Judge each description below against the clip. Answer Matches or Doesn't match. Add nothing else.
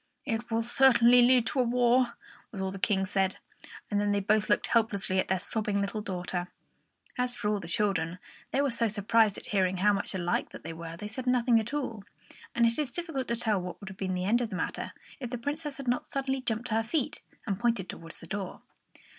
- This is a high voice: Matches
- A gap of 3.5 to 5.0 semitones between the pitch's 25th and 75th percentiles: Matches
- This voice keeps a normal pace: Doesn't match